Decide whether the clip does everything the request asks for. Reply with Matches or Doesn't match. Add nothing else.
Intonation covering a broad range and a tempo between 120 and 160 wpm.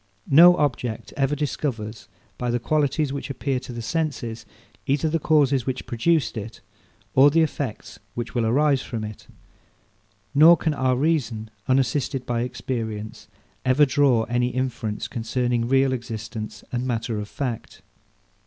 Doesn't match